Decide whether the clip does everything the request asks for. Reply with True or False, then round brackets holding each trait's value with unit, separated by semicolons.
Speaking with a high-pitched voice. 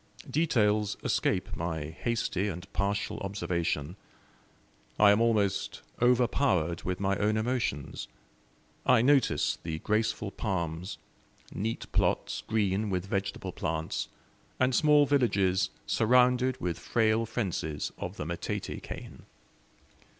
False (100 Hz)